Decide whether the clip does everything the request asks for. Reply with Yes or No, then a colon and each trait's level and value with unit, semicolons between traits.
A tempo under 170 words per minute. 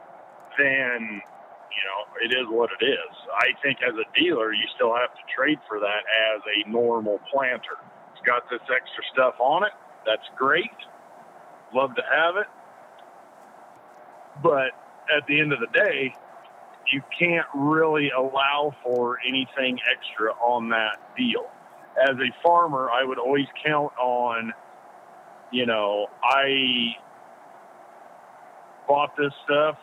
Yes: slow, 135 wpm